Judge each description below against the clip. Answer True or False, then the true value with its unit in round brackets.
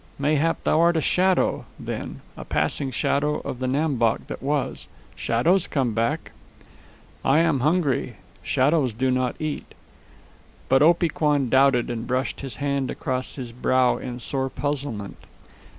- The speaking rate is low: False (150 wpm)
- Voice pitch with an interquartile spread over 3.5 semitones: False (2.9 semitones)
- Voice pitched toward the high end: False (135 Hz)